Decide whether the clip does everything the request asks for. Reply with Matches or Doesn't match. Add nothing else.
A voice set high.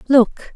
Matches